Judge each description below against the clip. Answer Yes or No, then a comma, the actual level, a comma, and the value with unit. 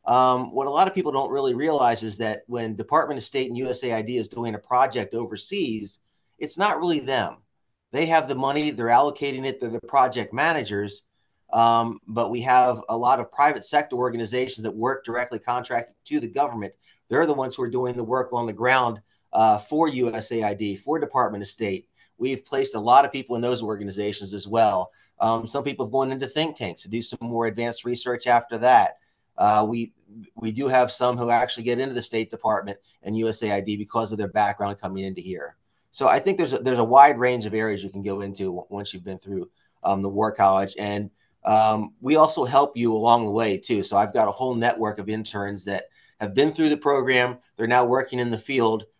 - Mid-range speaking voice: No, low, 115 Hz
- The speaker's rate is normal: No, fast, 215 wpm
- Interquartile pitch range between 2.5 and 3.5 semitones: Yes, average, 3.1 semitones